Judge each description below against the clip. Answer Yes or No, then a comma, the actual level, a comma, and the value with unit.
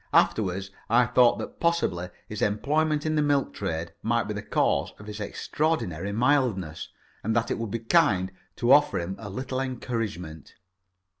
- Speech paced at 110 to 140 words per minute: No, average, 165 wpm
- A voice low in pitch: Yes, low, 115 Hz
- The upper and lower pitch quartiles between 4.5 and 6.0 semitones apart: Yes, wide, 5.6 semitones